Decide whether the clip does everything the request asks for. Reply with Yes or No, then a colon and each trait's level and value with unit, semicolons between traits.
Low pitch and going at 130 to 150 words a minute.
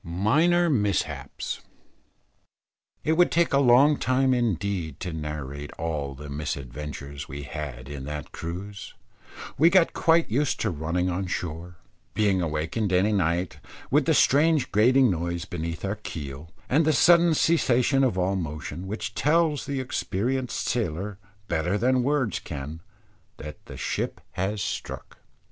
Yes: very low, 95 Hz; average, 140 wpm